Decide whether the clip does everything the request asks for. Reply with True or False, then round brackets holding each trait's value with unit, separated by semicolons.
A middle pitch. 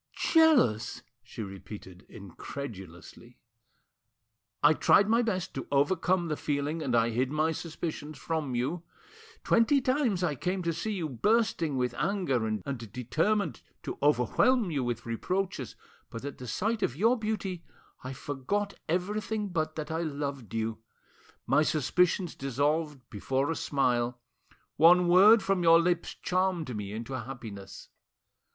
True (155 Hz)